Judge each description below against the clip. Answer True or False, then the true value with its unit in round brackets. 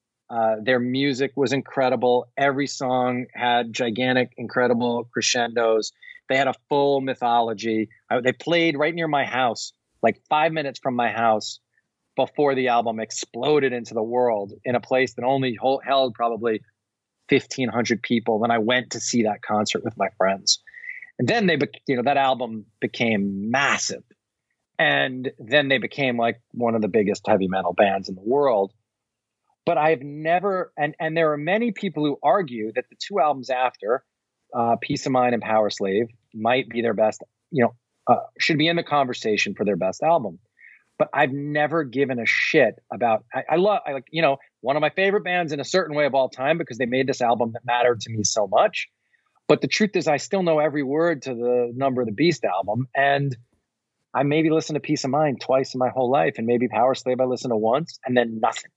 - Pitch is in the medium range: False (125 Hz)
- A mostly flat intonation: False (3.7 semitones)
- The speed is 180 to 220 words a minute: True (200 wpm)